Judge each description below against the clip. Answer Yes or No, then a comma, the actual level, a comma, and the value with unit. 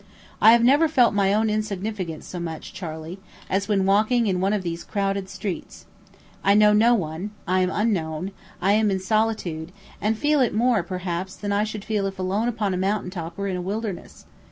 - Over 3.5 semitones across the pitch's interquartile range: No, average, 2.7 semitones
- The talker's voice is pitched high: Yes, high, 200 Hz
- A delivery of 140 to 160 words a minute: No, average, 200 wpm